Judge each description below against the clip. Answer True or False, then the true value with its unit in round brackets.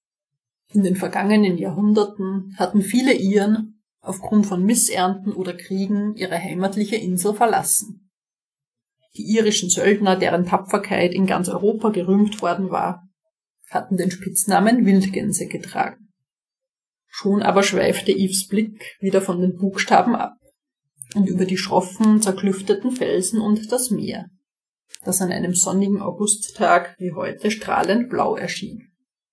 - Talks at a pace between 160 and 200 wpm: False (125 wpm)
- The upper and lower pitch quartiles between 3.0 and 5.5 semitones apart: False (2.4 semitones)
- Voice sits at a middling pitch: False (195 Hz)